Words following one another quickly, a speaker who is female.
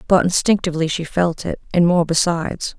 No: average, 175 wpm; female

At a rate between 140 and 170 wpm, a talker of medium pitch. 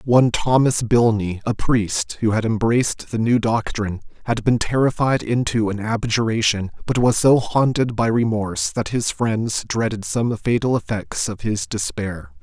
No: average, 160 wpm; low, 115 Hz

